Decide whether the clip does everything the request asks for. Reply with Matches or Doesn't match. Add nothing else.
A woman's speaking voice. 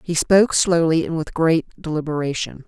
Matches